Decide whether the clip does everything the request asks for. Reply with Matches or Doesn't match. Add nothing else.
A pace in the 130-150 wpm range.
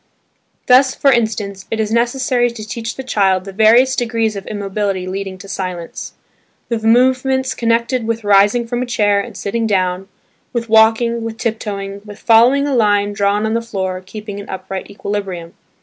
Doesn't match